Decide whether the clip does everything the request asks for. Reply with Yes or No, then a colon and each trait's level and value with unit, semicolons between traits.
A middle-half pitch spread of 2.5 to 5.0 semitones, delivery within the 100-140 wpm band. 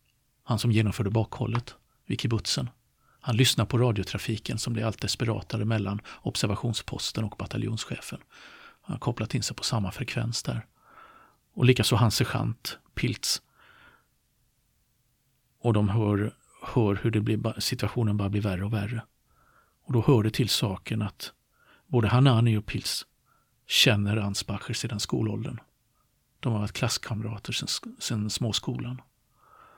Yes: average, 2.8 semitones; average, 135 wpm